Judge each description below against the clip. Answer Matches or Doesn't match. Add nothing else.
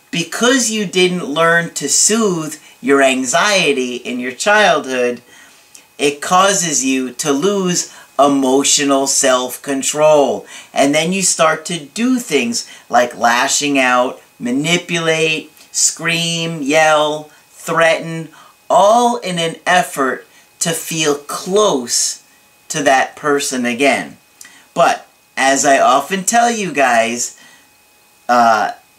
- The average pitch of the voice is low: Doesn't match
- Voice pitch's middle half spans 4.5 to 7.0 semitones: Matches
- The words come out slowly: Matches